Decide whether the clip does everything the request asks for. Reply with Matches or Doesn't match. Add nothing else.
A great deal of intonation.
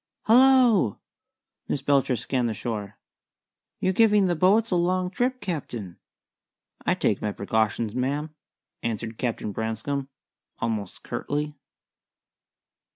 Matches